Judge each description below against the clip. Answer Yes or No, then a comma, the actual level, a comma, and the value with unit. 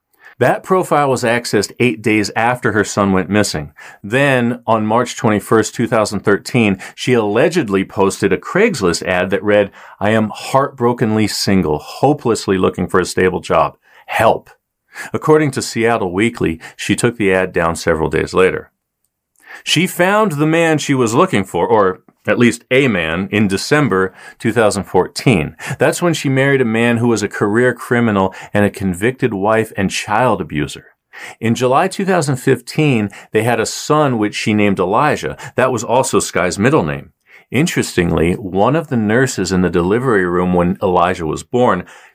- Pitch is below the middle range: Yes, low, 115 Hz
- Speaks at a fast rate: No, average, 160 wpm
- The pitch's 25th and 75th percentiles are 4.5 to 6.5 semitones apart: Yes, average, 4.8 semitones